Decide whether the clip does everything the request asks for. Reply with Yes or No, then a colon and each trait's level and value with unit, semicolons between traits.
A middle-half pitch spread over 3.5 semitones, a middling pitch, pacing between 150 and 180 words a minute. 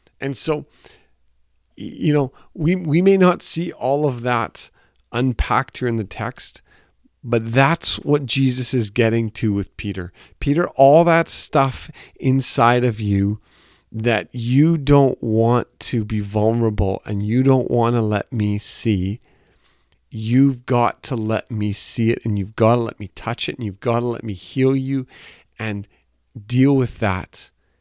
No: average, 4.2 semitones; low, 115 Hz; average, 160 wpm